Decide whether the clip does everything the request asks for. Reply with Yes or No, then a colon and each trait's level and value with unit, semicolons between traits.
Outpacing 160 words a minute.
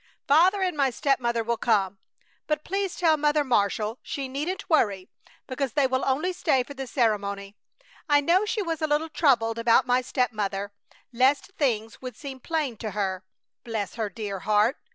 Yes: average, 175 wpm